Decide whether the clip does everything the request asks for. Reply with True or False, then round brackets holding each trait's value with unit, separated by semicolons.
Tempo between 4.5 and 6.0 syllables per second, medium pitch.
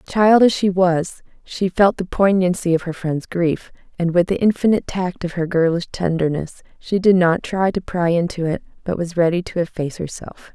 True (5.0 syllables/s; 175 Hz)